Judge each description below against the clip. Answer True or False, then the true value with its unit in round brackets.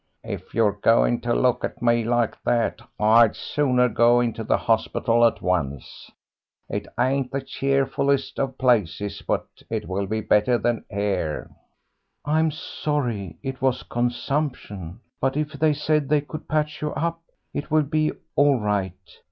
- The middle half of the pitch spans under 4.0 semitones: False (5.3 semitones)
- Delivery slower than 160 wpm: True (150 wpm)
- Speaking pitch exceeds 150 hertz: False (120 Hz)